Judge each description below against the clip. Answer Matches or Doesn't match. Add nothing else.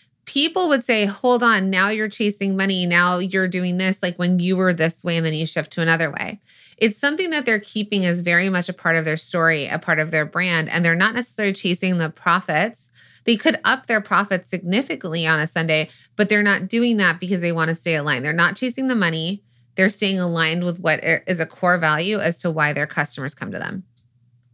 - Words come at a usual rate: Doesn't match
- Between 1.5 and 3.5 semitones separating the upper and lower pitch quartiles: Doesn't match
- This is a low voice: Doesn't match